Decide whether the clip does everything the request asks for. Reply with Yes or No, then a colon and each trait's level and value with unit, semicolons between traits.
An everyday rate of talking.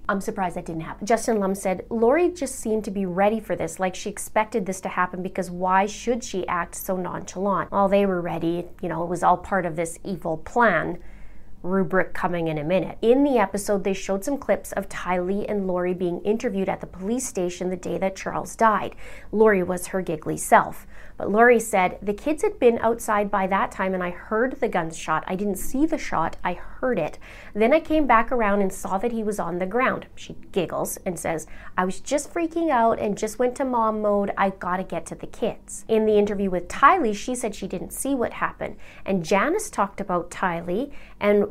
No: fast, 220 wpm